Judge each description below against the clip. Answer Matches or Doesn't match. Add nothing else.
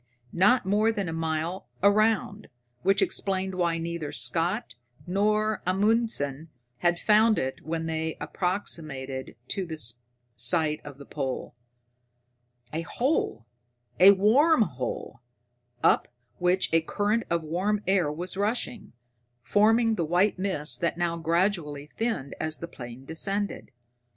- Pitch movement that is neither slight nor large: Matches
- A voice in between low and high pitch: Matches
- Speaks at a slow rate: Matches